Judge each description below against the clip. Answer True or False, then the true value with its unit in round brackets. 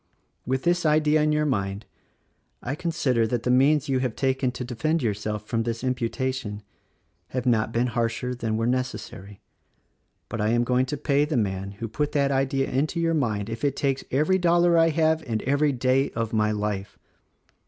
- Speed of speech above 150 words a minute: True (185 wpm)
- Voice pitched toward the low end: True (130 Hz)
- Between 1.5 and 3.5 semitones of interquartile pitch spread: False (4.5 semitones)